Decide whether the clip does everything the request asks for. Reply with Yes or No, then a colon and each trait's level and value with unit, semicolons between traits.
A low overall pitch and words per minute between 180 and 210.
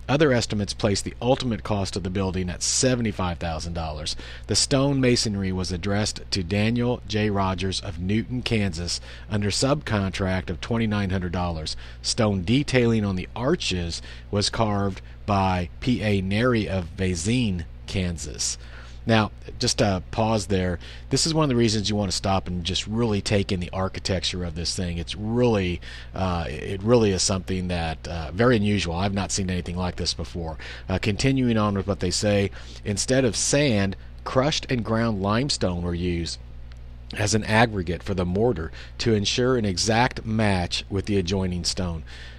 No: very low, 95 Hz; average, 165 wpm